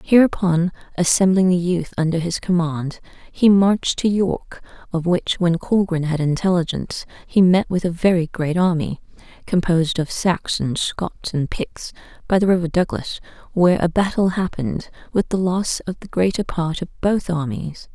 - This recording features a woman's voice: Yes, female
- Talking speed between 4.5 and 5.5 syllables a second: Yes, 4.8 syllables/s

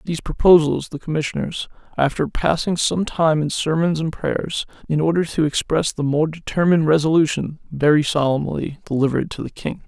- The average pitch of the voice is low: No, medium, 155 Hz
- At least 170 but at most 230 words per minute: No, average, 160 wpm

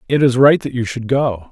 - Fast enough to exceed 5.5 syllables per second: No, 5.3 syllables/s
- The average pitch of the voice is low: Yes, low, 125 Hz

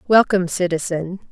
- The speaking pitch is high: No, medium, 180 Hz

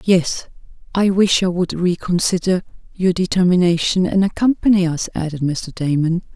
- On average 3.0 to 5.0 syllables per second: Yes, 4.9 syllables/s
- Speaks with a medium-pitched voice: Yes, medium, 180 Hz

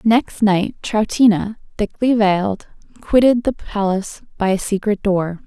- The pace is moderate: No, slow, 130 wpm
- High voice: Yes, high, 210 Hz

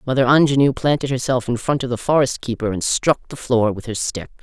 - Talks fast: Yes, fast, 230 wpm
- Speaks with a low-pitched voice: Yes, low, 125 Hz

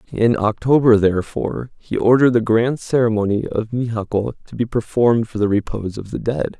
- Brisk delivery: No, average, 175 wpm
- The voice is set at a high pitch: No, low, 115 Hz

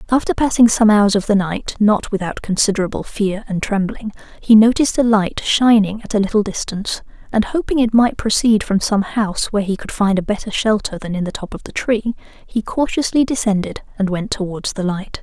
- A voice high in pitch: Yes, high, 210 Hz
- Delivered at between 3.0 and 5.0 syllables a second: No, 5.5 syllables/s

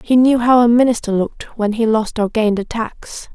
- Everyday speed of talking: No, fast, 235 wpm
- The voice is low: No, high, 225 Hz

